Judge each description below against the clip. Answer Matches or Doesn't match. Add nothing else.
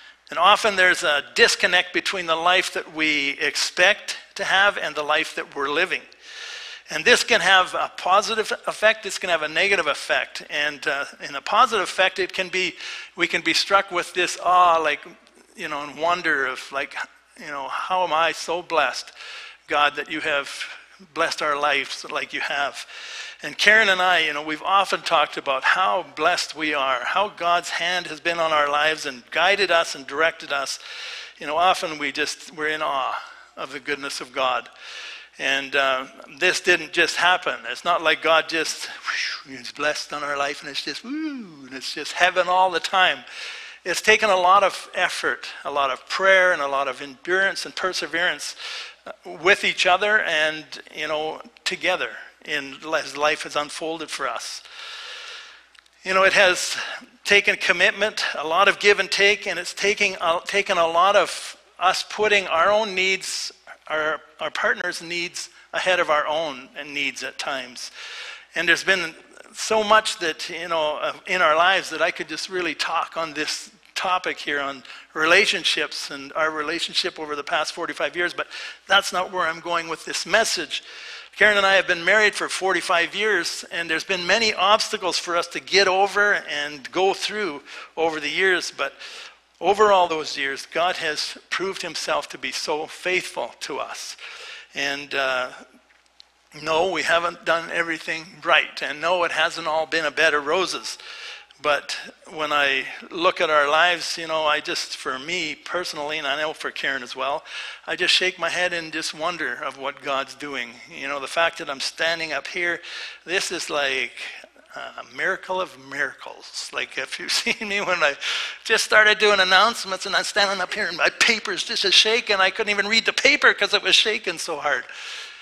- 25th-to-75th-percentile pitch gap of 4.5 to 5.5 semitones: Matches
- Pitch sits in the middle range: Matches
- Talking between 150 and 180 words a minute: Doesn't match